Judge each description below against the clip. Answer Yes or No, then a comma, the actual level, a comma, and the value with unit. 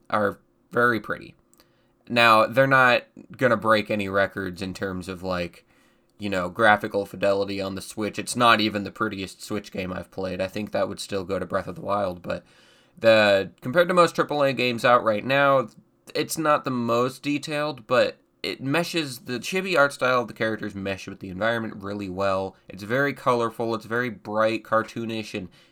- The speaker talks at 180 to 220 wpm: Yes, average, 190 wpm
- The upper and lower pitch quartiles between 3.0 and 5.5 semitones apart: Yes, average, 4.2 semitones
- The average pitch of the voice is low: Yes, low, 110 Hz